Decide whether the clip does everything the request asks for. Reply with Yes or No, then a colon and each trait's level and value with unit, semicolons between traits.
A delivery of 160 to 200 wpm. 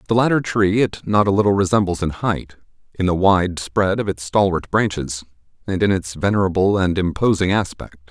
Yes: average, 185 wpm